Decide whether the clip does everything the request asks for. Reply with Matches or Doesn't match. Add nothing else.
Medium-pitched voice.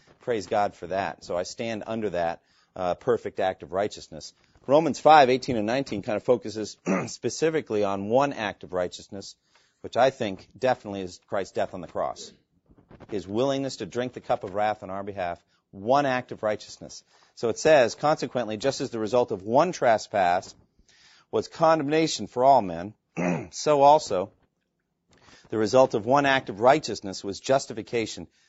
Doesn't match